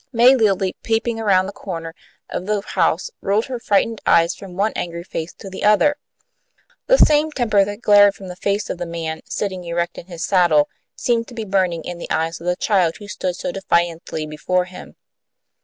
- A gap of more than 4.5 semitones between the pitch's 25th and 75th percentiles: No, average, 3.8 semitones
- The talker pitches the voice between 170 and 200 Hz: Yes, high, 190 Hz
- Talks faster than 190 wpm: Yes, average, 200 wpm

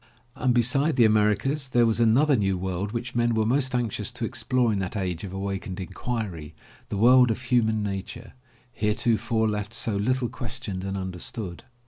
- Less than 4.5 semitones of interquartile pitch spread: Yes, average, 3.8 semitones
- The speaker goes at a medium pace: Yes, average, 175 wpm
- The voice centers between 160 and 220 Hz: No, low, 110 Hz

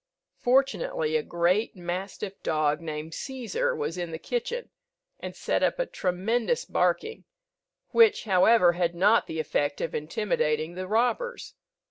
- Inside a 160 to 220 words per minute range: No, slow, 135 wpm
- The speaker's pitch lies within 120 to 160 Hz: No, high, 195 Hz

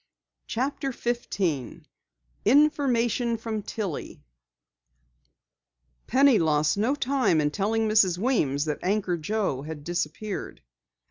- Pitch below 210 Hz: No, high, 215 Hz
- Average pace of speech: No, slow, 95 wpm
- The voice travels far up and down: Yes, wide, 7.0 semitones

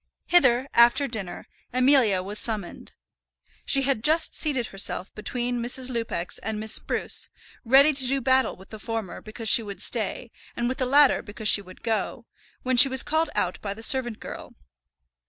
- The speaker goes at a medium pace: Yes, average, 175 wpm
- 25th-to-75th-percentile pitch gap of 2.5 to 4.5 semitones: Yes, average, 3.5 semitones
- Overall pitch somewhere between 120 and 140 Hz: No, high, 235 Hz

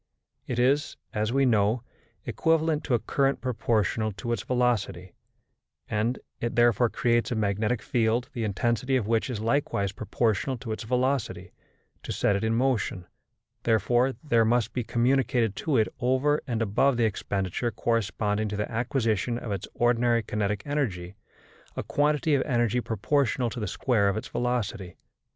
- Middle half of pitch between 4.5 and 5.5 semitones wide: No, average, 3.0 semitones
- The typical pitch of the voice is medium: No, low, 115 Hz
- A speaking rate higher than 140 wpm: Yes, average, 160 wpm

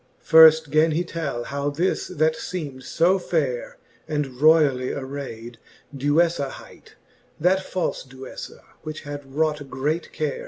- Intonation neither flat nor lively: Yes, average, 3.0 semitones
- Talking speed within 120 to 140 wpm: Yes, slow, 135 wpm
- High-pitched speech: No, medium, 150 Hz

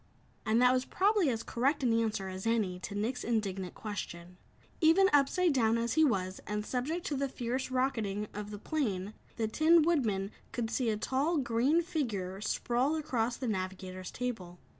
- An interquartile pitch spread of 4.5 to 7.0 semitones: Yes, average, 5.1 semitones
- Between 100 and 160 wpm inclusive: No, average, 175 wpm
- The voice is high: Yes, high, 235 Hz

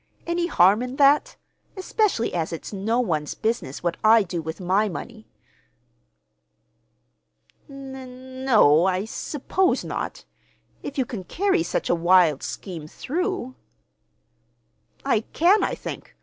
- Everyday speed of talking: No, slow, 120 wpm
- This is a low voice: No, high, 230 Hz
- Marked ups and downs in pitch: Yes, wide, 7.4 semitones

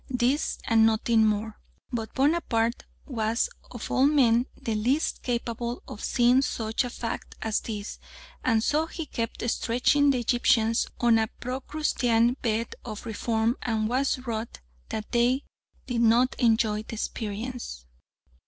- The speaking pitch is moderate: No, high, 235 Hz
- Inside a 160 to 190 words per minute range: No, average, 140 wpm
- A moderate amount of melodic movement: No, narrow, 2.2 semitones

